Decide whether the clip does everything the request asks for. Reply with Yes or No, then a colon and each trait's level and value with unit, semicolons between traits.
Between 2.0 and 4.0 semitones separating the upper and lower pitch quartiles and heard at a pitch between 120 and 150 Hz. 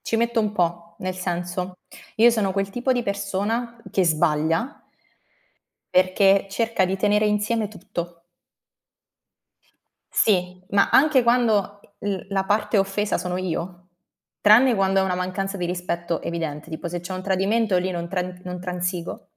No: average, 2.7 semitones; high, 190 Hz